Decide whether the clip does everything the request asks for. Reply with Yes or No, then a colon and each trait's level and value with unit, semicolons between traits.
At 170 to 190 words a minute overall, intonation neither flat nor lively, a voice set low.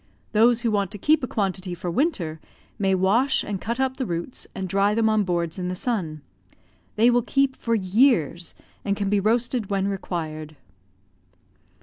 No: average, 185 wpm; average, 4.6 semitones; high, 200 Hz